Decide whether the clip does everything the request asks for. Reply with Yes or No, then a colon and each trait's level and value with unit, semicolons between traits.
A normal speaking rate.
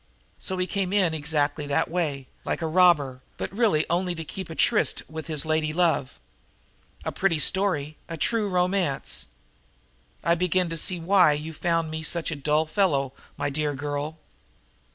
Yes: average, 170 wpm